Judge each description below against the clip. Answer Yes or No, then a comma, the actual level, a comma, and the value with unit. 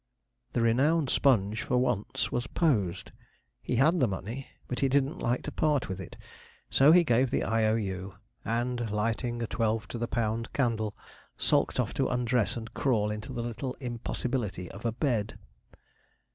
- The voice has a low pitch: Yes, low, 120 Hz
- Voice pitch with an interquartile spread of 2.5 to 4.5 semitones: Yes, average, 3.0 semitones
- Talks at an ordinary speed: Yes, average, 165 wpm